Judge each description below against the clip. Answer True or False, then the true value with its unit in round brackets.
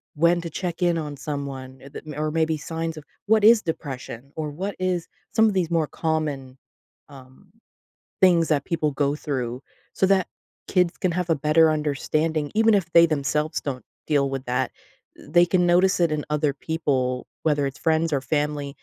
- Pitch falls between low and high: True (155 Hz)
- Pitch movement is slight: False (3.2 semitones)